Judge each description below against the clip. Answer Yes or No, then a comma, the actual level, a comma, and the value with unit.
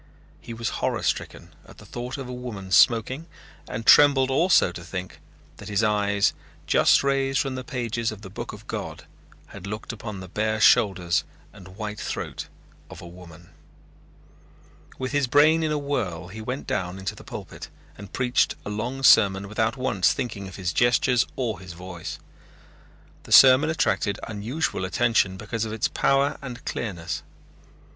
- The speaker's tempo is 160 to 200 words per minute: Yes, average, 165 wpm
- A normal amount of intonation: Yes, average, 5.0 semitones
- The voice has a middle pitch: No, low, 110 Hz